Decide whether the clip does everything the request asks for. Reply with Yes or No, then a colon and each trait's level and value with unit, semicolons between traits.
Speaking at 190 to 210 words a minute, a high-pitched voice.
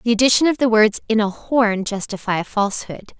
Yes: fast, 205 wpm; high, 220 Hz